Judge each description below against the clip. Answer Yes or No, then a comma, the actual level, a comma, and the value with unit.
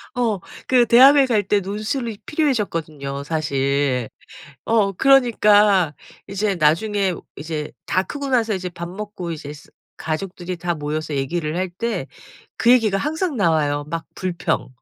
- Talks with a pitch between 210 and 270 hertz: No, medium, 185 Hz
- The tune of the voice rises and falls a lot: Yes, wide, 6.1 semitones